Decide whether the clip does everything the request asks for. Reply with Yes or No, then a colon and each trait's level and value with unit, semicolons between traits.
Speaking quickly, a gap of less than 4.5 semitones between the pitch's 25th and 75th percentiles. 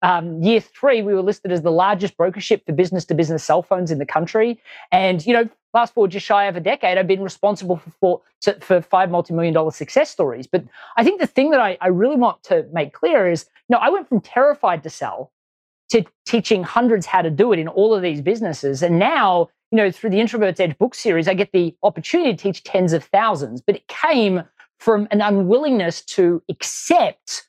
No: fast, 220 wpm; average, 4.9 semitones